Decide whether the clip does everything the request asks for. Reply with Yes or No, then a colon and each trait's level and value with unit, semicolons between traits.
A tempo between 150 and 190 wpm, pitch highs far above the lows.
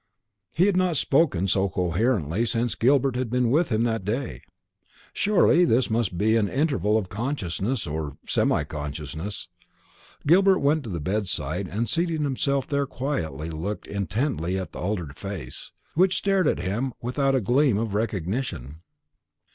Yes: average, 155 wpm; wide, 7.0 semitones